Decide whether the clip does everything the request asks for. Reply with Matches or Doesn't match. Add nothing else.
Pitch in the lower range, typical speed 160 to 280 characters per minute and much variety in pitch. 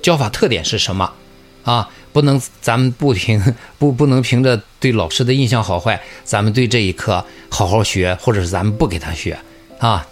Matches